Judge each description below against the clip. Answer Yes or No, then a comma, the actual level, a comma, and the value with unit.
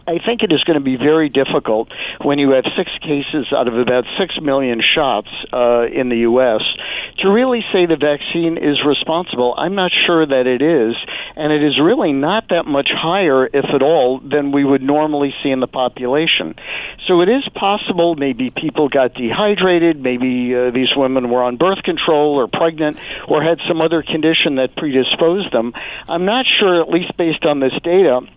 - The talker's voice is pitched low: No, medium, 150 Hz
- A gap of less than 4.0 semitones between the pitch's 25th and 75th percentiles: No, average, 4.5 semitones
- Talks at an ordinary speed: Yes, average, 190 wpm